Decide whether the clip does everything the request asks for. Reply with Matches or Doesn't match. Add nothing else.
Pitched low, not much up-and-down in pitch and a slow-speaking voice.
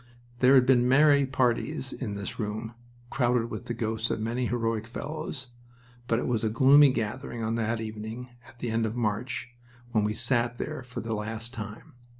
Doesn't match